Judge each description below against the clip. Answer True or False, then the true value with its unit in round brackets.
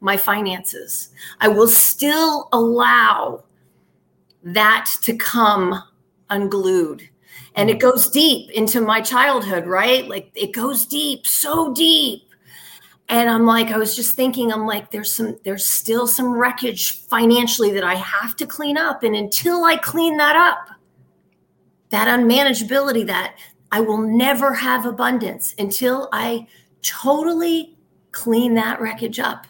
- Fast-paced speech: False (135 wpm)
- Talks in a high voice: True (230 Hz)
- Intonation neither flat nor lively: True (4.2 semitones)